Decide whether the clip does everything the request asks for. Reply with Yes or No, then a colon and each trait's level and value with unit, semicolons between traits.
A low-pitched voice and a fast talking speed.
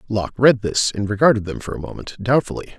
Yes: low, 110 Hz; fast, 215 wpm